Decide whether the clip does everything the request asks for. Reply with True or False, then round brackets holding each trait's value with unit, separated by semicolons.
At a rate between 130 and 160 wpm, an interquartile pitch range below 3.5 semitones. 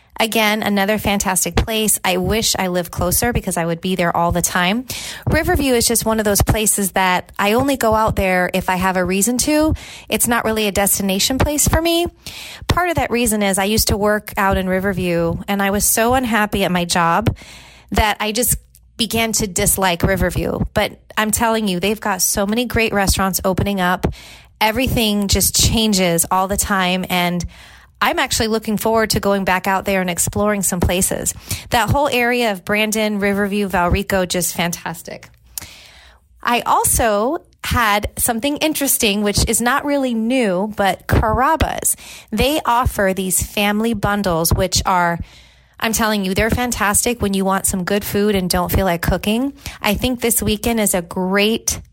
False (180 wpm; 3.0 semitones)